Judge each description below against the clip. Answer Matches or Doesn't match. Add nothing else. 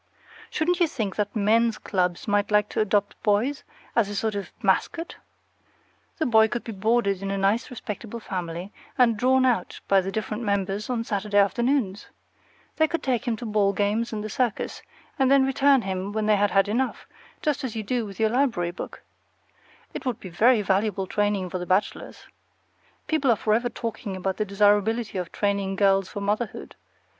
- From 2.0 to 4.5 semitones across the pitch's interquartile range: Matches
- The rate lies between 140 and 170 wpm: Doesn't match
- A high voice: Matches